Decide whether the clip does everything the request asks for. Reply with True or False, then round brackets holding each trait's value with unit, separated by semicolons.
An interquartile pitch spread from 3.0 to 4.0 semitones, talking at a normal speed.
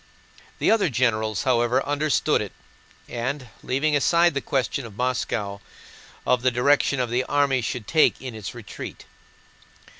True (3.3 semitones; 145 wpm)